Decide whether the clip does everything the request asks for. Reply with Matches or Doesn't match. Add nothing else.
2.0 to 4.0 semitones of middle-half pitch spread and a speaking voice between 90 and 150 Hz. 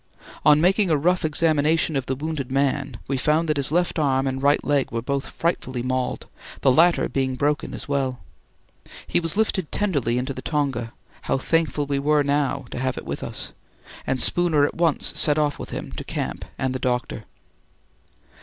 Matches